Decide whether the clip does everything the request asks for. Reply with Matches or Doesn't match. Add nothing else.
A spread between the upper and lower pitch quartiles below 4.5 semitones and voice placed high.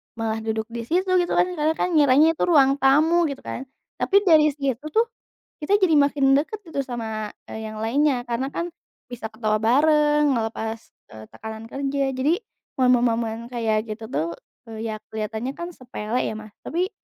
Doesn't match